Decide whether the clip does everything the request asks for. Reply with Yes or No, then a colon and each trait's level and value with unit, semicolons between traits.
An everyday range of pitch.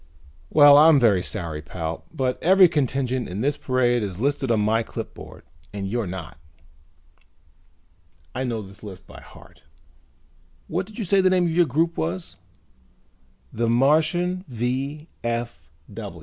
No: wide, 7.2 semitones